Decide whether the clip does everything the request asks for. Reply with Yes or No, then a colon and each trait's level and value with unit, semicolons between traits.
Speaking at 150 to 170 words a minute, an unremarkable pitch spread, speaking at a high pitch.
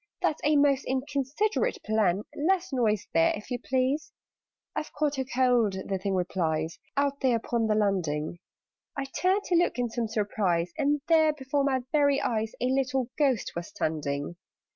No: average, 165 wpm; wide, 6.0 semitones; very high, 255 Hz